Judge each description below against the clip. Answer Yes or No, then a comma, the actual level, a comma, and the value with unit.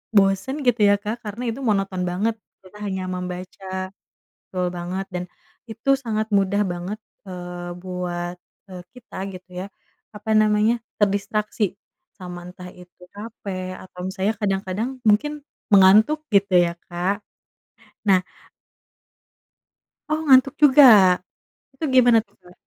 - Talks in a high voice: Yes, high, 195 Hz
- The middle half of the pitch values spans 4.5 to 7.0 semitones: No, average, 3.3 semitones